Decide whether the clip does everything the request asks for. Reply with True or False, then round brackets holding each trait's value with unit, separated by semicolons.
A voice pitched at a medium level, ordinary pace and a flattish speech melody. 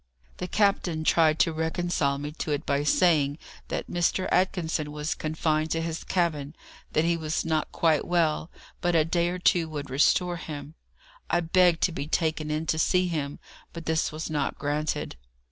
True (160 Hz; 180 wpm; 2.1 semitones)